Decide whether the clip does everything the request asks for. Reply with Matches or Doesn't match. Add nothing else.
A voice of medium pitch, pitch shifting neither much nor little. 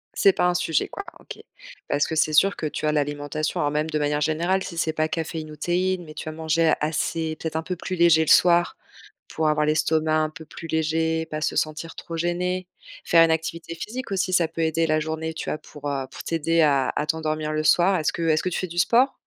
Doesn't match